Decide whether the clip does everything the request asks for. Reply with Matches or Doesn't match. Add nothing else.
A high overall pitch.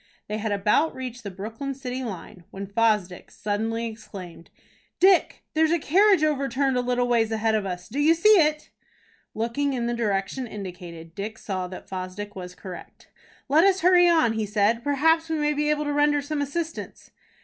Matches